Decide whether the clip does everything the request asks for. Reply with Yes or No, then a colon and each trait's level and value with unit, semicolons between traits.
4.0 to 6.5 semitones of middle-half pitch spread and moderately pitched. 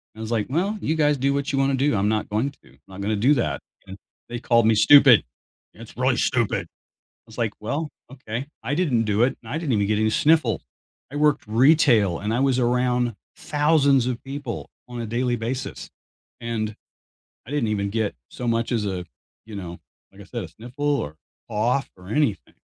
No: average, 4.3 semitones; low, 120 Hz